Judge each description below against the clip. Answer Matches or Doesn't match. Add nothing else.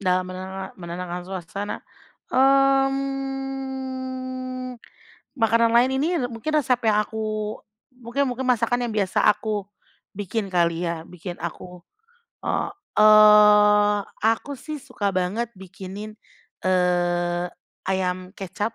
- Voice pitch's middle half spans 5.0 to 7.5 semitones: Matches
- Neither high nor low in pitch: Doesn't match